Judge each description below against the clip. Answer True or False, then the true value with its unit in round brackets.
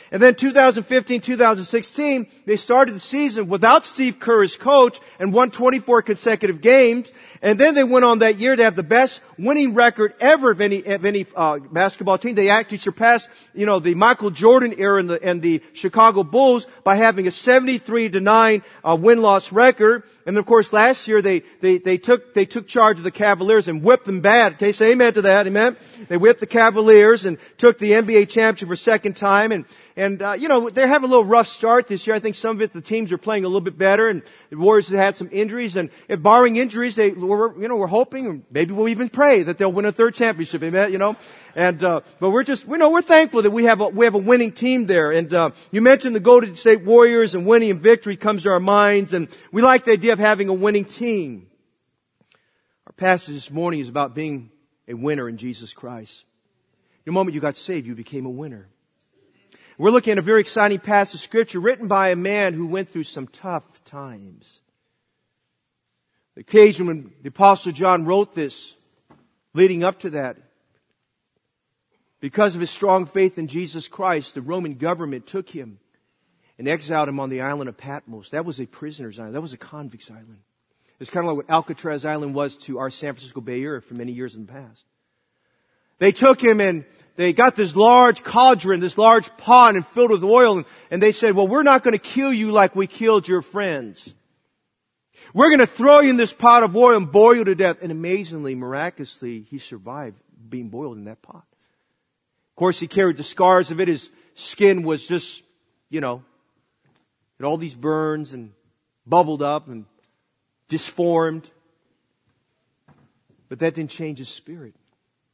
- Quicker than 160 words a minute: True (205 wpm)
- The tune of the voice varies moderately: False (5.9 semitones)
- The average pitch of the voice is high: True (195 Hz)